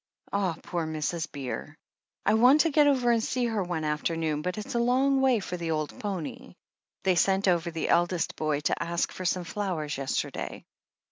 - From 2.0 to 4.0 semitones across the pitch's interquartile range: No, wide, 5.6 semitones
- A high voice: No, medium, 180 Hz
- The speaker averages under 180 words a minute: No, average, 190 wpm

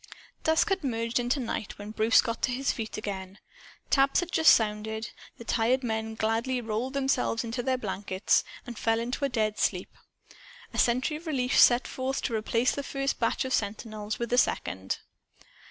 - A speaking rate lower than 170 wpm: No, average, 175 wpm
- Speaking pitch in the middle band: No, high, 235 Hz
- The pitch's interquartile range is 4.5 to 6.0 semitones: No, average, 3.1 semitones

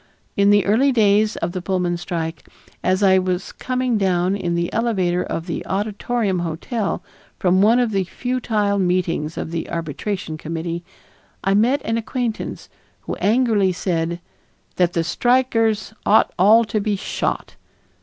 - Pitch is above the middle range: Yes, high, 195 Hz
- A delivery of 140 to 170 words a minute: Yes, average, 150 wpm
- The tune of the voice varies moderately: Yes, average, 4.0 semitones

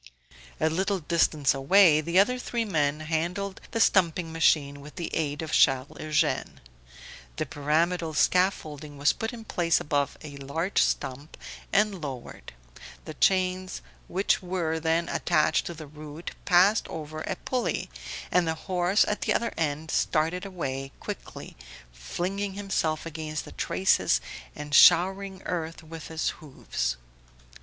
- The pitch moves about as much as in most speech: Yes, average, 3.8 semitones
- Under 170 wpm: Yes, average, 140 wpm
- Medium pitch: Yes, medium, 160 Hz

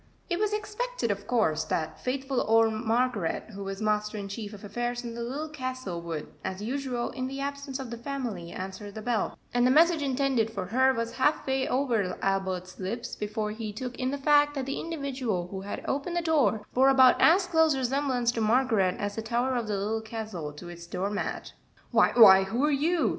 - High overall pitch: Yes, high, 235 Hz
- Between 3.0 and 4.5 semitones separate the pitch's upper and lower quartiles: No, average, 4.9 semitones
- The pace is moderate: No, fast, 210 wpm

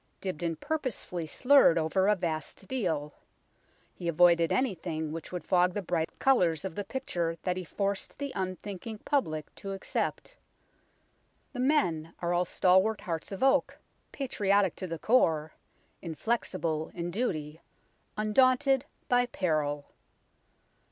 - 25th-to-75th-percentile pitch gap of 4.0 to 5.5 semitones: Yes, average, 5.2 semitones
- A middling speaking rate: No, slow, 130 wpm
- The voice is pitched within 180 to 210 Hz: Yes, medium, 185 Hz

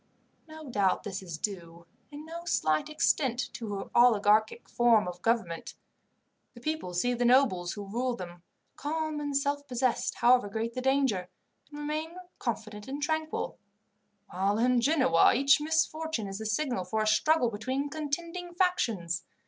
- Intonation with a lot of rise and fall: Yes, wide, 6.3 semitones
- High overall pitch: Yes, high, 245 Hz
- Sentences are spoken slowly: No, average, 155 wpm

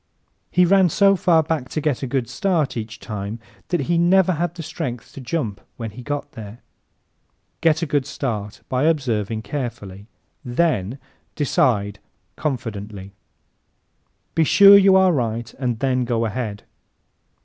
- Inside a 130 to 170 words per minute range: Yes, average, 150 wpm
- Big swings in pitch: Yes, wide, 6.7 semitones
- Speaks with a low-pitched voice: Yes, low, 130 Hz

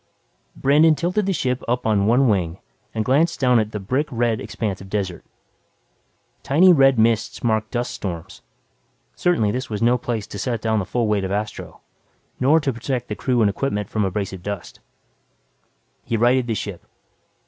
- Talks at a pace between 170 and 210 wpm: Yes, average, 175 wpm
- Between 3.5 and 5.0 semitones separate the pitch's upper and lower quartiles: Yes, average, 3.9 semitones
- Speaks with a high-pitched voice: No, low, 115 Hz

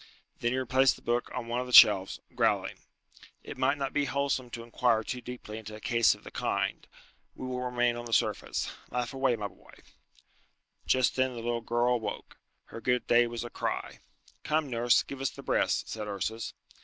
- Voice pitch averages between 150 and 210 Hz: No, low, 120 Hz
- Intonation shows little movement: Yes, narrow, 1.7 semitones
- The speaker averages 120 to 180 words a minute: No, average, 200 wpm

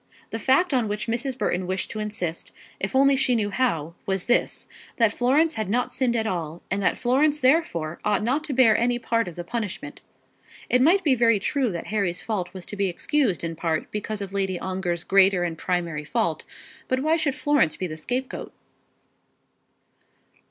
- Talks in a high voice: Yes, high, 215 Hz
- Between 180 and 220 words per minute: Yes, average, 190 wpm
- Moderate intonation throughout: No, wide, 6.1 semitones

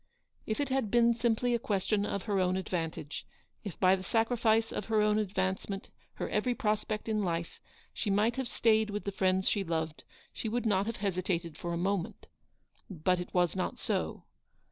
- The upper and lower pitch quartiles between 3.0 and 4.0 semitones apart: Yes, average, 3.3 semitones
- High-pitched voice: Yes, high, 205 Hz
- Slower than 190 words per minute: No, average, 195 wpm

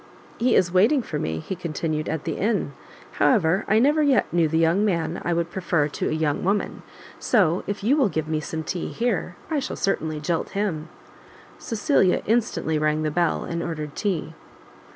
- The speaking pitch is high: No, medium, 175 Hz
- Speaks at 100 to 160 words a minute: No, average, 190 wpm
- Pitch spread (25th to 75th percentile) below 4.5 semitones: No, average, 4.9 semitones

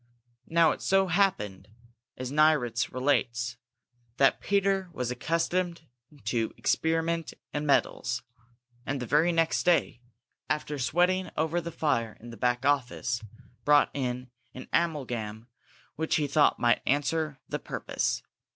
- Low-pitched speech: No, medium, 145 Hz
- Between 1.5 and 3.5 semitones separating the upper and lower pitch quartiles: No, average, 5.1 semitones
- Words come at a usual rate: No, slow, 130 wpm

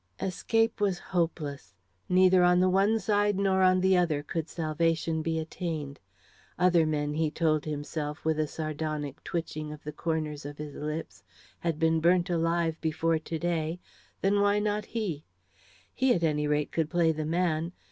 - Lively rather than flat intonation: No, average, 2.9 semitones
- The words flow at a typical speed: Yes, average, 165 wpm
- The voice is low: No, medium, 165 Hz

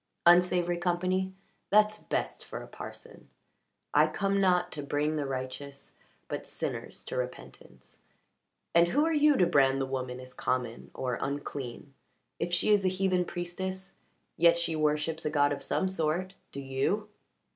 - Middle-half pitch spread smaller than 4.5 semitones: No, average, 5.1 semitones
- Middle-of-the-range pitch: Yes, medium, 170 Hz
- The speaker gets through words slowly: No, average, 155 wpm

